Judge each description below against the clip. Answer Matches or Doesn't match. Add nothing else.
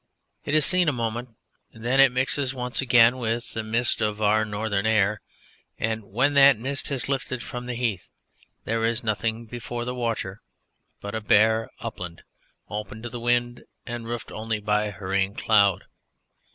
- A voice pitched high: Doesn't match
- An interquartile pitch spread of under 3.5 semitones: Matches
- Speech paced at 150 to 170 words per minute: Matches